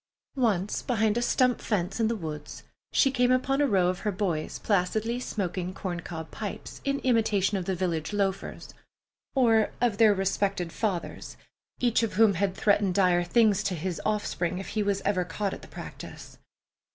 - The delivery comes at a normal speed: Yes, average, 175 wpm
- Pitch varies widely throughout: No, average, 3.6 semitones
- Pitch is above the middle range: Yes, high, 200 Hz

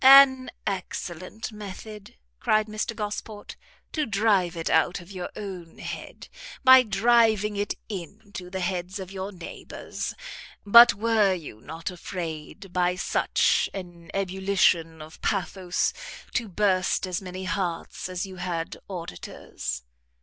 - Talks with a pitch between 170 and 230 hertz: Yes, high, 190 Hz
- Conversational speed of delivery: No, slow, 130 wpm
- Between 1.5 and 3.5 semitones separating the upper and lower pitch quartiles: Yes, average, 3.0 semitones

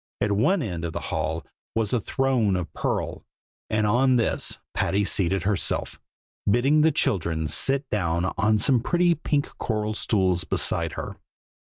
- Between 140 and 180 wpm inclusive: Yes, average, 155 wpm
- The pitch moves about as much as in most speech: No, wide, 6.0 semitones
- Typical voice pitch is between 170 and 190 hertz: No, low, 105 Hz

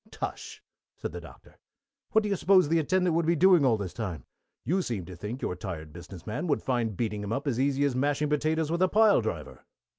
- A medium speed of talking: No, fast, 230 wpm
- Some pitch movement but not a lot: No, wide, 8.5 semitones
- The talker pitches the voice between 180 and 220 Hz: No, medium, 140 Hz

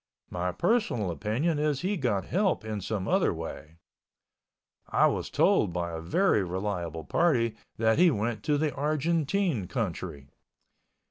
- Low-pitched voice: Yes, low, 110 Hz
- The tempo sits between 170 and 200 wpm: No, average, 140 wpm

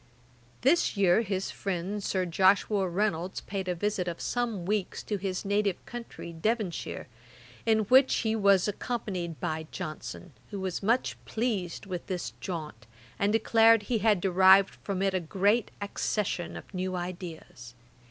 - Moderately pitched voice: No, high, 195 Hz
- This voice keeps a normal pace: Yes, average, 150 wpm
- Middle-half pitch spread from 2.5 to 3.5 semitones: Yes, average, 2.9 semitones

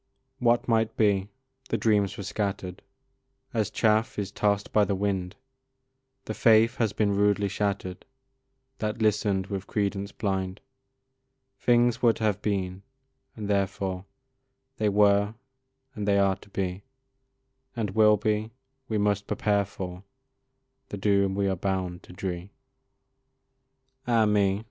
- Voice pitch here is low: Yes, low, 100 Hz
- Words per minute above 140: No, slow, 135 wpm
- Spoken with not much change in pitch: Yes, narrow, 1.7 semitones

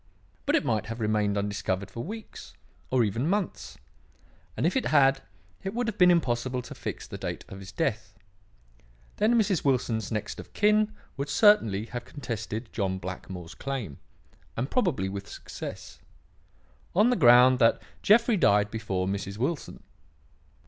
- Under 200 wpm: Yes, average, 155 wpm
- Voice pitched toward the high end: No, low, 120 Hz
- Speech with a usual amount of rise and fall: No, wide, 8.9 semitones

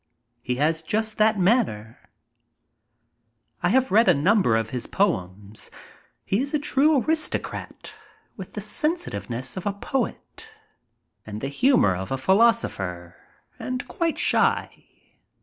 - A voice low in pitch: No, high, 190 Hz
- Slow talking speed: Yes, slow, 130 wpm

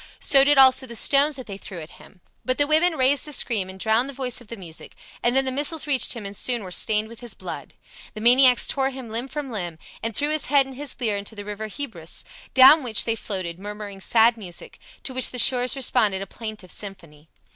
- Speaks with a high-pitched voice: Yes, high, 235 Hz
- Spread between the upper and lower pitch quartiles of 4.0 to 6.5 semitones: Yes, average, 4.8 semitones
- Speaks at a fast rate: Yes, fast, 235 wpm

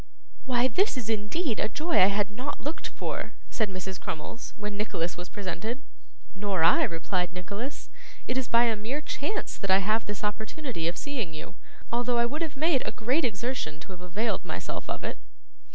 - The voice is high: Yes, high, 220 Hz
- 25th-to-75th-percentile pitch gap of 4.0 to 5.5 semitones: Yes, average, 5.2 semitones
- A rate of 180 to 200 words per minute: Yes, average, 190 wpm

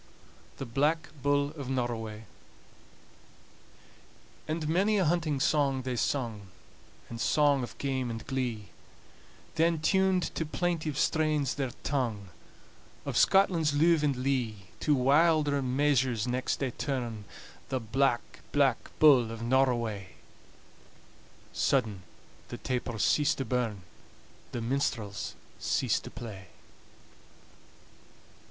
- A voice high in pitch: No, low, 135 Hz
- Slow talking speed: Yes, slow, 110 wpm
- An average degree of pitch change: Yes, average, 4.2 semitones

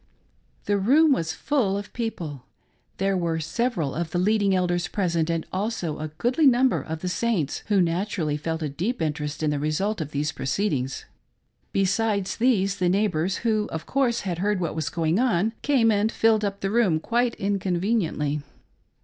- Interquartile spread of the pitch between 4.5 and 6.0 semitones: Yes, wide, 5.4 semitones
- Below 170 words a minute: No, average, 175 wpm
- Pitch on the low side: No, high, 190 Hz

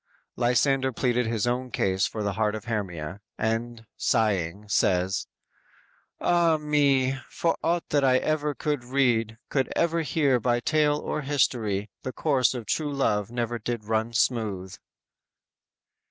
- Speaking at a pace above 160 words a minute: No, average, 140 wpm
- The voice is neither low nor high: No, low, 120 Hz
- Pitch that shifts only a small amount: No, average, 4.4 semitones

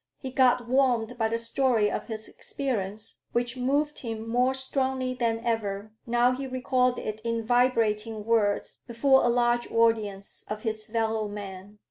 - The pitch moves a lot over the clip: No, narrow, 2.6 semitones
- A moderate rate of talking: Yes, average, 155 wpm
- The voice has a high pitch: Yes, high, 230 Hz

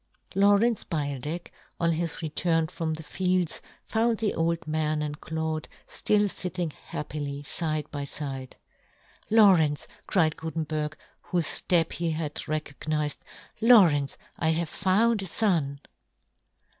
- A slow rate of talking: Yes, slow, 130 wpm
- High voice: No, medium, 160 Hz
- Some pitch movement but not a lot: Yes, average, 3.3 semitones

